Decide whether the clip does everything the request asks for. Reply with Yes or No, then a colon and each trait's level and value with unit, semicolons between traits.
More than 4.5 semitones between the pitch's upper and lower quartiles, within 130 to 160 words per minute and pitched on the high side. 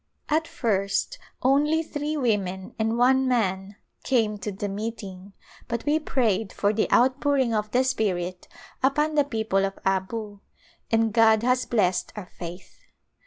Yes: average, 4.9 semitones; average, 145 wpm; high, 225 Hz